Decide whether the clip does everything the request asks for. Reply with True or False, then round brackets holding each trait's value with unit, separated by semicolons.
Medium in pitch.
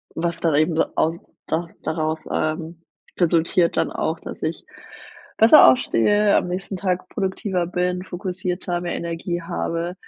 True (175 Hz)